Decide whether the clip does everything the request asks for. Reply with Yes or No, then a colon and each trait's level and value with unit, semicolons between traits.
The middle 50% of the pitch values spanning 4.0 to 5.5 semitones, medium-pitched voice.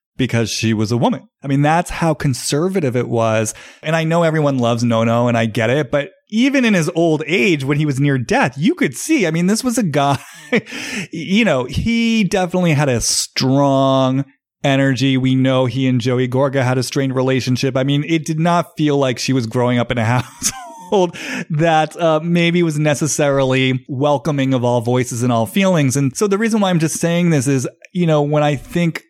Yes: average, 4.8 semitones; medium, 145 Hz